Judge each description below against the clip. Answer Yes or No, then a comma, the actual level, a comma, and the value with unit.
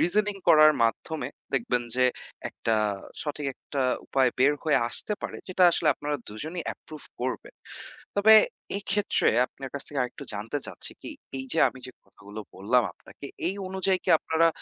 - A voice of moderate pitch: Yes, medium, 145 Hz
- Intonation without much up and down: No, wide, 5.5 semitones